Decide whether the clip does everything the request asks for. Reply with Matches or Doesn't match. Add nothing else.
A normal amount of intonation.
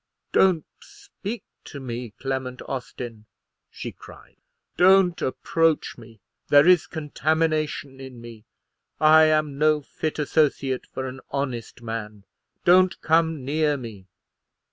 Matches